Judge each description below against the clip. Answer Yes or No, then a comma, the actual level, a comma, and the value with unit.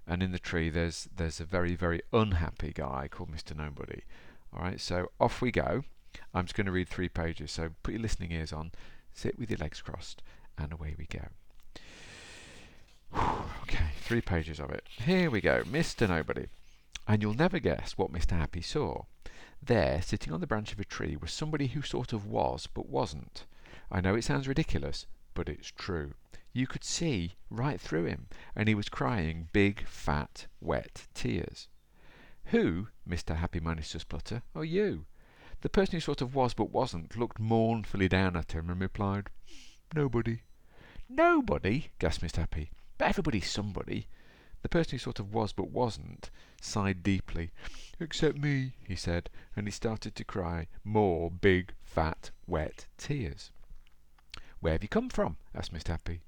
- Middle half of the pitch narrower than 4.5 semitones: No, wide, 5.6 semitones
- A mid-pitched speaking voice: No, very low, 95 Hz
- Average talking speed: Yes, average, 170 wpm